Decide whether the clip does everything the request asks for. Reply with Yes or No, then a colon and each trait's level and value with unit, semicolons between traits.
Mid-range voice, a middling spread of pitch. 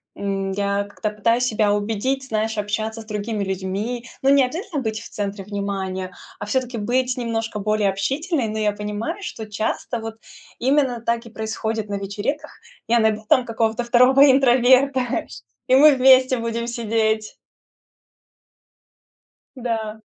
No: high, 225 Hz; average, 3.2 semitones